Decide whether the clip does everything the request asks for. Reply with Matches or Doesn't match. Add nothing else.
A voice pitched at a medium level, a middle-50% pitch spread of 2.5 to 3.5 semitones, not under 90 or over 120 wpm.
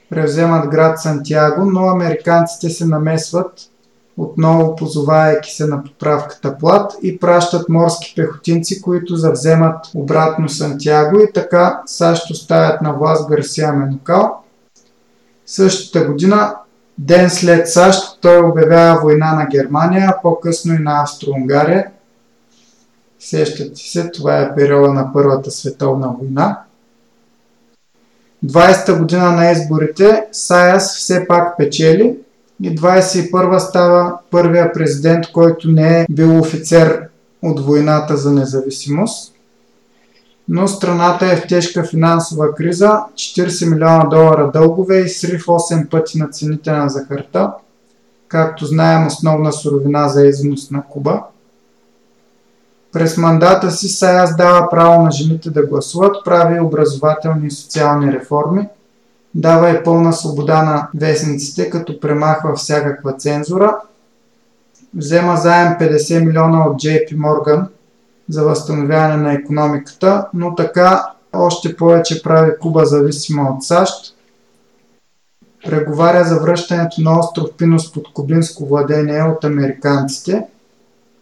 Matches